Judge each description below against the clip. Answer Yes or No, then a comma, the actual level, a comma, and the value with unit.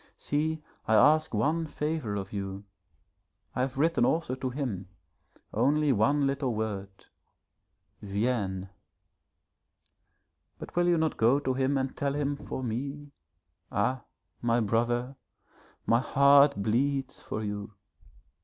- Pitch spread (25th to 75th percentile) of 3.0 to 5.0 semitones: Yes, average, 4.7 semitones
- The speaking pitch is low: Yes, low, 130 Hz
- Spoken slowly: Yes, slow, 125 wpm